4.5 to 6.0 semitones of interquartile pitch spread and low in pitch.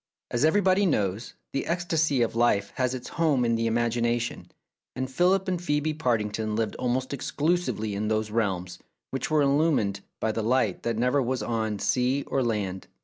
Yes: average, 5.0 semitones; low, 120 Hz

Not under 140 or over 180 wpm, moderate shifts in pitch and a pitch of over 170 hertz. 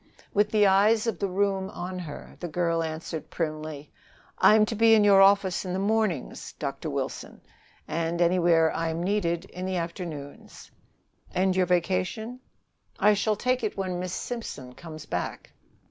Yes: average, 160 wpm; average, 3.5 semitones; medium, 185 Hz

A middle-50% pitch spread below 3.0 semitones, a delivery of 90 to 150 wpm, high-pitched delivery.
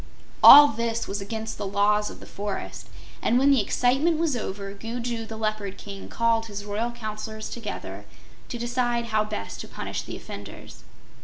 No: narrow, 2.4 semitones; average, 170 wpm; high, 220 Hz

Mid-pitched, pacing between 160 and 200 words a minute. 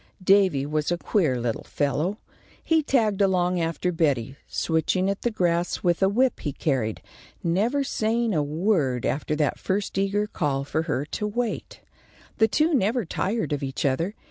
Yes: medium, 180 Hz; average, 170 wpm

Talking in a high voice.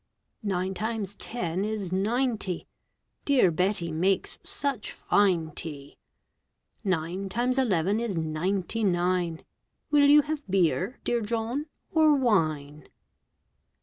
Yes: high, 195 Hz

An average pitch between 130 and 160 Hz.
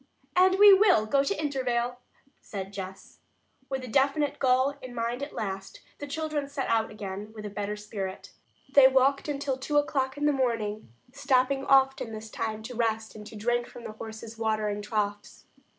No: high, 240 Hz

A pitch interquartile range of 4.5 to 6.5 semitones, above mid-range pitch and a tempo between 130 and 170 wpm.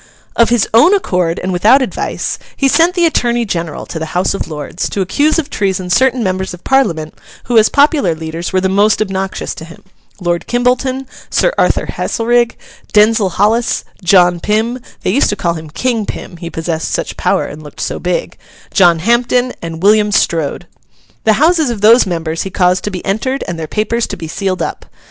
No: wide, 5.6 semitones; high, 200 Hz; average, 195 wpm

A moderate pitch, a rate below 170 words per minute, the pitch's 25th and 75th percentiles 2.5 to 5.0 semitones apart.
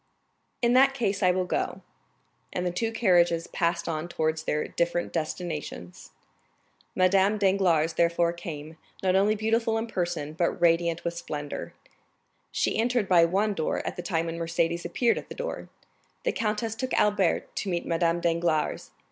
Yes: medium, 175 Hz; average, 160 wpm; average, 3.7 semitones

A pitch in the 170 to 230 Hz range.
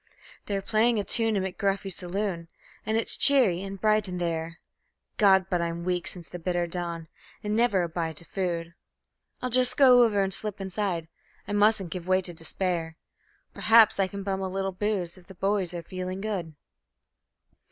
Yes: high, 190 Hz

